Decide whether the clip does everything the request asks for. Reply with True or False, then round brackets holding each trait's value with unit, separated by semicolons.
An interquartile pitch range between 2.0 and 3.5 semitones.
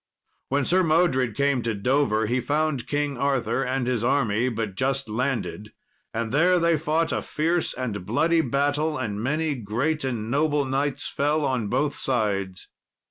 False (4.3 semitones)